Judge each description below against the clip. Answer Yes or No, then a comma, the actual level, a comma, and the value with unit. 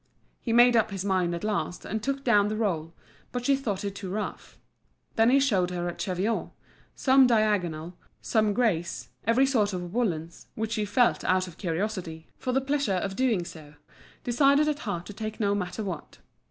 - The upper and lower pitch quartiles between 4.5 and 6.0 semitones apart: Yes, average, 5.0 semitones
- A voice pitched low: No, high, 210 Hz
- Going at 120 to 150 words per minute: No, average, 190 wpm